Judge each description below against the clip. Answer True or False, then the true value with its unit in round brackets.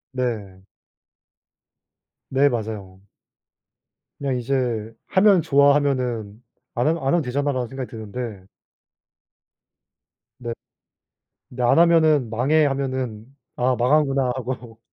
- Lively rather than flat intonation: False (3.6 semitones)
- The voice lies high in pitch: False (125 Hz)